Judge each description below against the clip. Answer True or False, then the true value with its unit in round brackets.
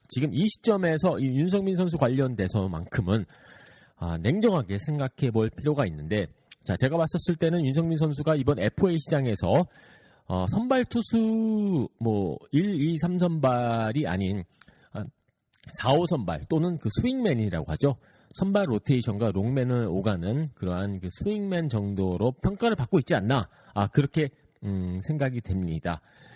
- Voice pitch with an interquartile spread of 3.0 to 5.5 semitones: False (8.0 semitones)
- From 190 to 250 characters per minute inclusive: False (280 characters per minute)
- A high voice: False (135 Hz)